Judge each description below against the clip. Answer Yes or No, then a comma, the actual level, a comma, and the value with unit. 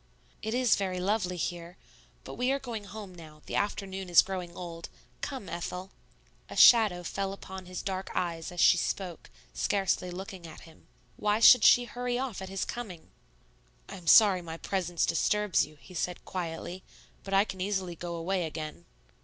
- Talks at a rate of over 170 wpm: Yes, average, 180 wpm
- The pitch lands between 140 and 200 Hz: Yes, medium, 185 Hz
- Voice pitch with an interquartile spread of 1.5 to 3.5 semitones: Yes, average, 2.8 semitones